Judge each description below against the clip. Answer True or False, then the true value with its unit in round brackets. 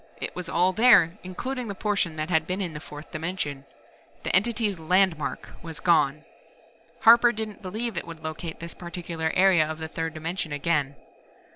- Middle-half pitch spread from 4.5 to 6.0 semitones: False (3.5 semitones)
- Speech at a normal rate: True (170 wpm)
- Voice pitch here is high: False (170 Hz)